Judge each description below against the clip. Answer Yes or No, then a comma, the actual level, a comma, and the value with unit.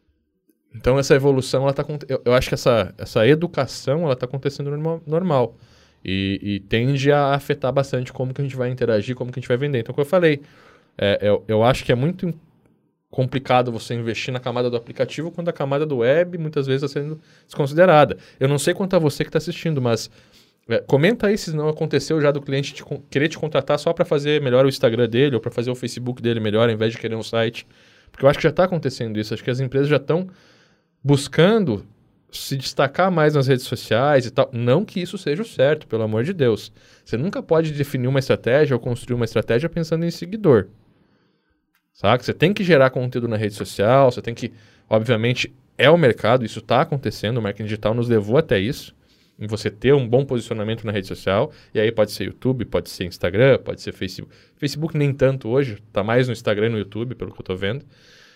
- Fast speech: Yes, fast, 220 wpm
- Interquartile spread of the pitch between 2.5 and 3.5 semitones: No, average, 4.4 semitones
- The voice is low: Yes, low, 130 Hz